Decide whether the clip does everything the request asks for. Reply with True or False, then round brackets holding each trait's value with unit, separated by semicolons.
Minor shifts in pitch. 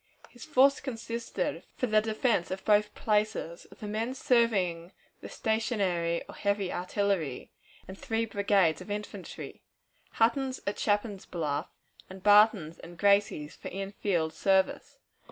False (3.7 semitones)